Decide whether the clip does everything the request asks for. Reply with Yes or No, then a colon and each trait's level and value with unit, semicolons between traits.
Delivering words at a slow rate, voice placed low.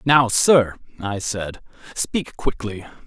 Yes: slow, 115 wpm; low, 115 Hz